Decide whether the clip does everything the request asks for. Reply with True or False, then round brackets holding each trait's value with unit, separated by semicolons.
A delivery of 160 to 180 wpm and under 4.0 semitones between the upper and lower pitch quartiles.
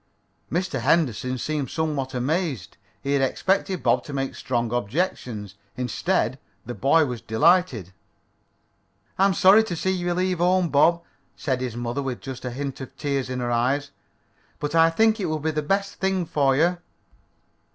False (170 wpm; 5.6 semitones)